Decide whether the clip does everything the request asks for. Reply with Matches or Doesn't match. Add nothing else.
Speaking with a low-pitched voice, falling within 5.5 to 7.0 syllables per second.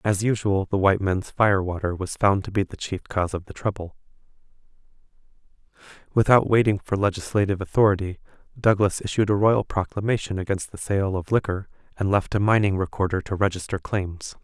Matches